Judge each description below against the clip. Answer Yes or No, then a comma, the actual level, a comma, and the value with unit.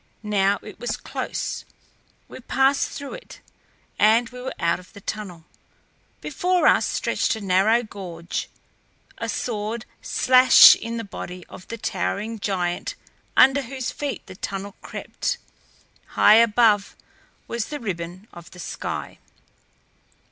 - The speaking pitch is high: Yes, high, 215 Hz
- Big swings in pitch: No, average, 4.2 semitones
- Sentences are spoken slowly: Yes, slow, 130 wpm